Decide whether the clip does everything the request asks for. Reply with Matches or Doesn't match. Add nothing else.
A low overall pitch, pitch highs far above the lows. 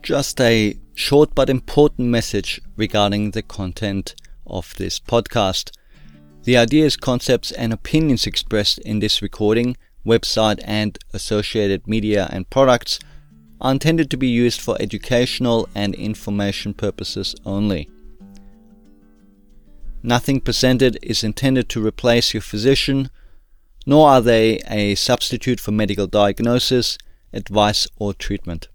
Doesn't match